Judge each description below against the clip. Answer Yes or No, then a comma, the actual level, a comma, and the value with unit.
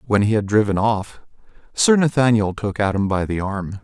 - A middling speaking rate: Yes, average, 190 wpm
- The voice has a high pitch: No, low, 105 Hz